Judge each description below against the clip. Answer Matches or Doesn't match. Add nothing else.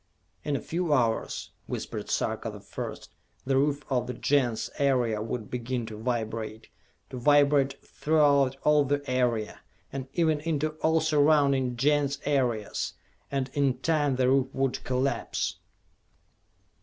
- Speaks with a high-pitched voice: Doesn't match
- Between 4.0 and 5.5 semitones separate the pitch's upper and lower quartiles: Doesn't match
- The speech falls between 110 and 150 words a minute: Matches